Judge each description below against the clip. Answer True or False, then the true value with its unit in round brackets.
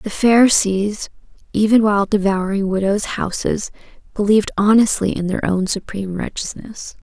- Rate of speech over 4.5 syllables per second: True (5.0 syllables/s)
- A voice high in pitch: True (205 Hz)